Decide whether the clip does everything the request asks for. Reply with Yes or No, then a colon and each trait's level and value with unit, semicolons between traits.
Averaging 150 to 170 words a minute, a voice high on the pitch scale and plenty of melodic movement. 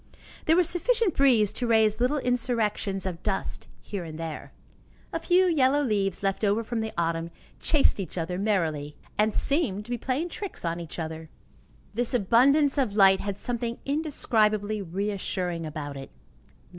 Yes: average, 160 wpm; high, 215 Hz; wide, 5.9 semitones